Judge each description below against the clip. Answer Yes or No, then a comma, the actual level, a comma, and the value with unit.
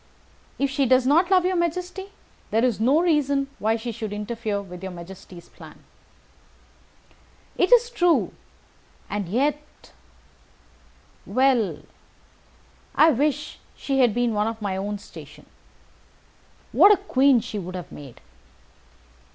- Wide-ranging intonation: Yes, wide, 6.4 semitones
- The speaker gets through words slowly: Yes, slow, 125 wpm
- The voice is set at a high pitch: Yes, very high, 250 Hz